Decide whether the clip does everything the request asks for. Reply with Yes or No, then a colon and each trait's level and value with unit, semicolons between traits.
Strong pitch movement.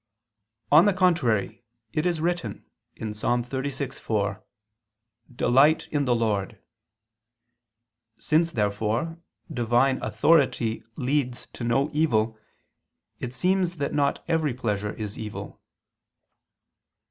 Yes: wide, 5.7 semitones